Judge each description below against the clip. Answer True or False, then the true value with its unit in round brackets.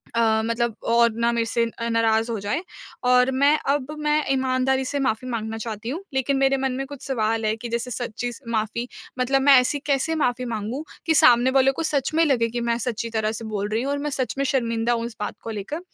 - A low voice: False (245 Hz)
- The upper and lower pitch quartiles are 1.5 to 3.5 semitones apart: True (3.0 semitones)